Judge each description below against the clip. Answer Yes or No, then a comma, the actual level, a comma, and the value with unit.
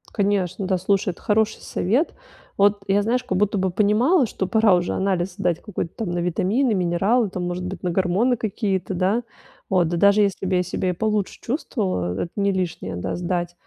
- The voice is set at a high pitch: Yes, high, 195 Hz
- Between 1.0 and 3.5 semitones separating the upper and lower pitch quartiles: Yes, average, 2.9 semitones